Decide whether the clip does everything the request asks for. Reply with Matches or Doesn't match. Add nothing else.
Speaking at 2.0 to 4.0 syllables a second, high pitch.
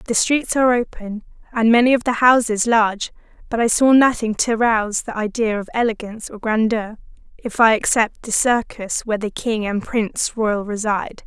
Doesn't match